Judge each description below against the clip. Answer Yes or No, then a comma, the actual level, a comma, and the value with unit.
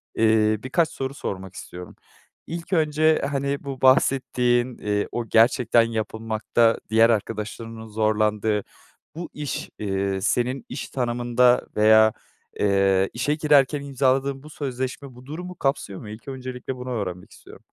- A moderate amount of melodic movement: Yes, average, 4.0 semitones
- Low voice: Yes, low, 120 Hz